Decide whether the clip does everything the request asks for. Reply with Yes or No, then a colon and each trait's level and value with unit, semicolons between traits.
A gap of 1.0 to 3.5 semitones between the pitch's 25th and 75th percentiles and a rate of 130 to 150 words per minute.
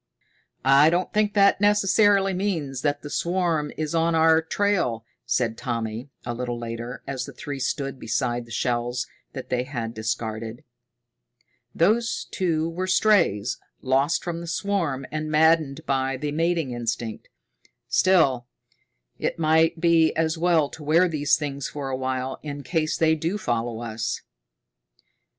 No: average, 5.2 semitones; average, 145 wpm